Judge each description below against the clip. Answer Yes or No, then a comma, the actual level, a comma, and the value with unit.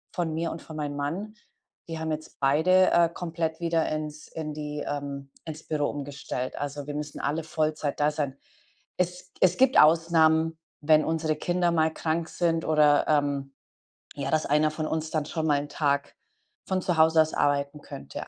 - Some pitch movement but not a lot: No, narrow, 1.9 semitones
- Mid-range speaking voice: Yes, medium, 155 Hz